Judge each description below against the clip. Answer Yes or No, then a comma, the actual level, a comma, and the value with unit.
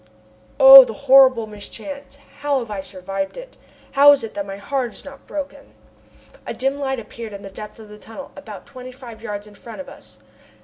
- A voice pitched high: Yes, high, 230 Hz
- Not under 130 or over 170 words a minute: No, fast, 205 wpm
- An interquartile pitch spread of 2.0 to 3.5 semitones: No, average, 4.8 semitones